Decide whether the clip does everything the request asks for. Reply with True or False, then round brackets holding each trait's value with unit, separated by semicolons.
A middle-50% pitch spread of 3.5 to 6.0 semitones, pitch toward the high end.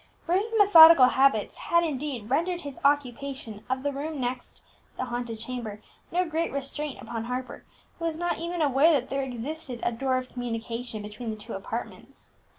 True (4.7 semitones; 265 Hz)